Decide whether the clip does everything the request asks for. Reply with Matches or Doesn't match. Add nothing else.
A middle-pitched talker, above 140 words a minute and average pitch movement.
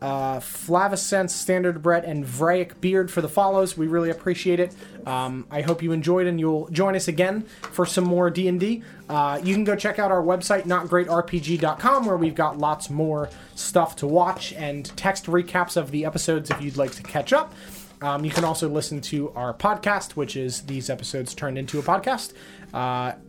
Matches